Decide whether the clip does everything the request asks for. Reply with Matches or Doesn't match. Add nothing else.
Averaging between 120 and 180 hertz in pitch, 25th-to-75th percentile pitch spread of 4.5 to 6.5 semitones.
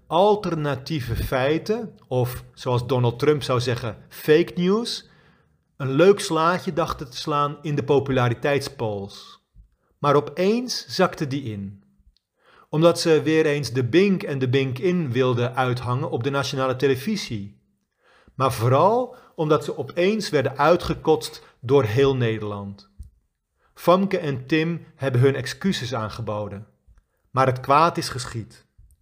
Matches